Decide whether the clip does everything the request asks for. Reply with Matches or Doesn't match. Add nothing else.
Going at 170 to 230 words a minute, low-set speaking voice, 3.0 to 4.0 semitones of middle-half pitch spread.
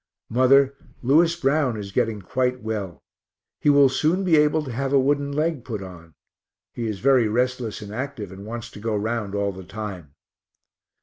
Doesn't match